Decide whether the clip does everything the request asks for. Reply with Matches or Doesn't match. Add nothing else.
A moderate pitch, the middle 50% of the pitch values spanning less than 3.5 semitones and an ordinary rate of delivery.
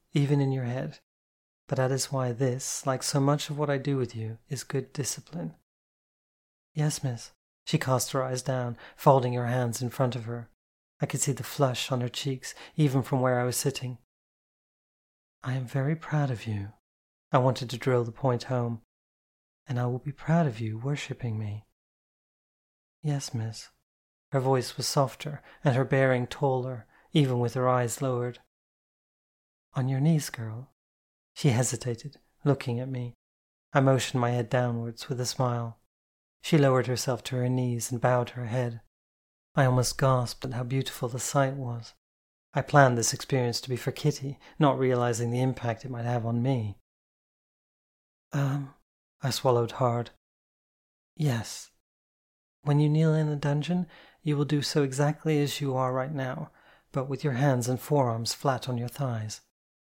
Doesn't match